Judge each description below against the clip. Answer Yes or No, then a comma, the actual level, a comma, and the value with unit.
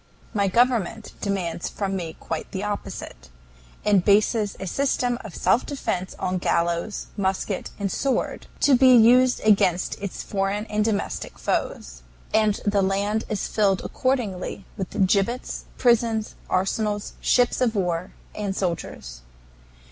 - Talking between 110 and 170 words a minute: Yes, slow, 135 wpm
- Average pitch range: Yes, average, 3.0 semitones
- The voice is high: Yes, high, 200 Hz